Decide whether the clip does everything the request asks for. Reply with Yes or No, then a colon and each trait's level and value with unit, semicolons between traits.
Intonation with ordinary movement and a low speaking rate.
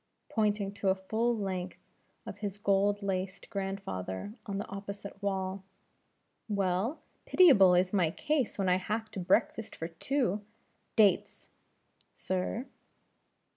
No: narrow, 2.0 semitones; slow, 125 wpm